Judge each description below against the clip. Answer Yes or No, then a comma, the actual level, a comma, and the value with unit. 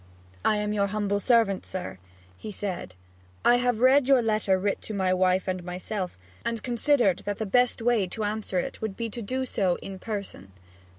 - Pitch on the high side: Yes, high, 205 Hz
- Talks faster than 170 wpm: Yes, average, 190 wpm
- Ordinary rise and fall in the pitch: Yes, average, 3.6 semitones